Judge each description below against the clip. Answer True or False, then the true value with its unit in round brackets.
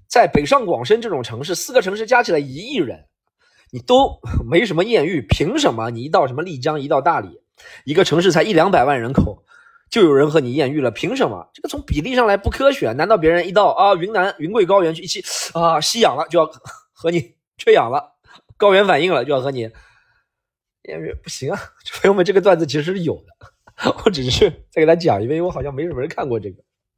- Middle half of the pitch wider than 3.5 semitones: True (5.6 semitones)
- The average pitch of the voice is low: False (165 Hz)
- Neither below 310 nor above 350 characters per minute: True (325 characters per minute)